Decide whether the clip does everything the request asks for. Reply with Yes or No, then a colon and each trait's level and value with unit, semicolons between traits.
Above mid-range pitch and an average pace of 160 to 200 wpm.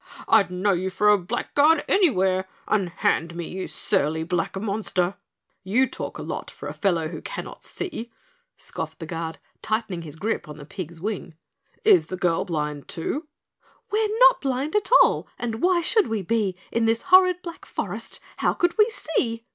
Yes: high, 210 Hz; average, 175 wpm